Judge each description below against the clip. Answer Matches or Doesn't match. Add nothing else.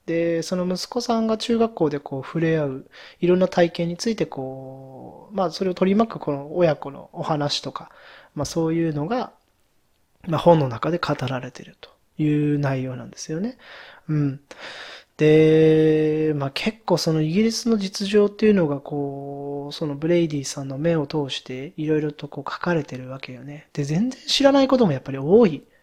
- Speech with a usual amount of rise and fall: Matches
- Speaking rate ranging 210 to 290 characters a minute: Doesn't match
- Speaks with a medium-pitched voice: Matches